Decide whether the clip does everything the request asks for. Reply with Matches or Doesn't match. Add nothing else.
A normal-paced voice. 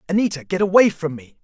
Doesn't match